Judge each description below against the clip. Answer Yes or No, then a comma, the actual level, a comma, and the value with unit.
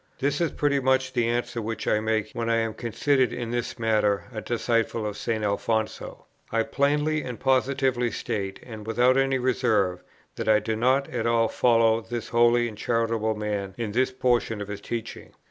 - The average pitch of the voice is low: Yes, low, 115 Hz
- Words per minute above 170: Yes, average, 185 wpm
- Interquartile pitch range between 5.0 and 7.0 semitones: No, average, 2.7 semitones